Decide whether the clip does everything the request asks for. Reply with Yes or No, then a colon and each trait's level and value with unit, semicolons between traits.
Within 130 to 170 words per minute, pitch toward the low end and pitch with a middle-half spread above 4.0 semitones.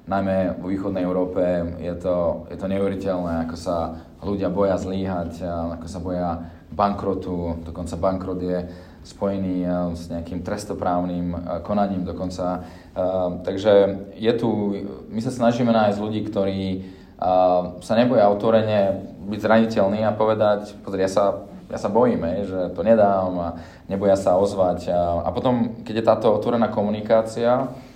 No: slow, 135 wpm; very low, 95 Hz; narrow, 2.6 semitones